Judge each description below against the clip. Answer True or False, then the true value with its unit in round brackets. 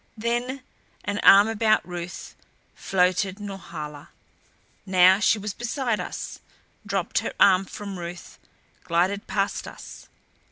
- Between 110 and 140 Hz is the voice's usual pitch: False (195 Hz)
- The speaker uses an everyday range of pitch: True (3.1 semitones)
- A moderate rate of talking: False (115 wpm)